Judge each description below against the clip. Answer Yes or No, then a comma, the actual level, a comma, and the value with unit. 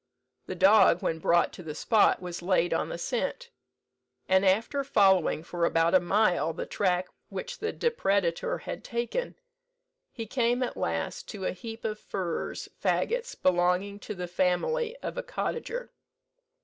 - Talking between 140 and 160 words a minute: Yes, average, 155 wpm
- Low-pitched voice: No, high, 195 Hz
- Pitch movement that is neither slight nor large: No, wide, 5.9 semitones